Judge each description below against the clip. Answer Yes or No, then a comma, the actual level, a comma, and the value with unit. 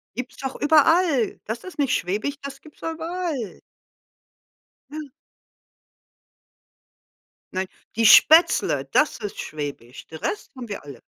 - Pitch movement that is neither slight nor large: No, wide, 7.3 semitones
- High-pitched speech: Yes, very high, 270 Hz